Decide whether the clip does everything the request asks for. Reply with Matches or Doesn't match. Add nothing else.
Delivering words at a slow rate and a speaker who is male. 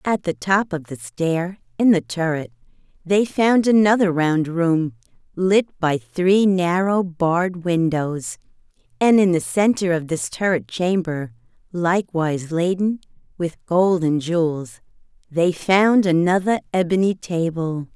Doesn't match